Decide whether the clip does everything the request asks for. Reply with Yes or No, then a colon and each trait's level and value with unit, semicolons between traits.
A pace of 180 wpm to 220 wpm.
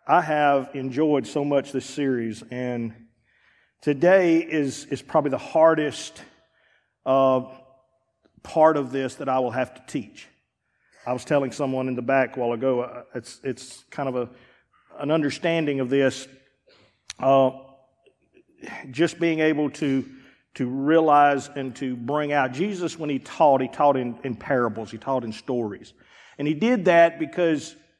No: average, 155 wpm